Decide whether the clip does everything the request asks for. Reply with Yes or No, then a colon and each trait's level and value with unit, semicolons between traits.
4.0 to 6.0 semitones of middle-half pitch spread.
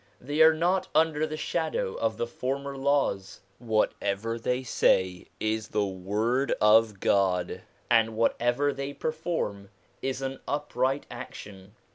Yes: average, 5.1 semitones